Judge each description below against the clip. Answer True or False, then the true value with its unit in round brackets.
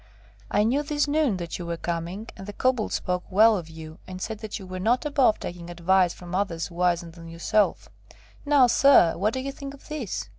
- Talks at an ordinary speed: False (215 wpm)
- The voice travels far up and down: True (6.6 semitones)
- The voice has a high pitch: True (195 Hz)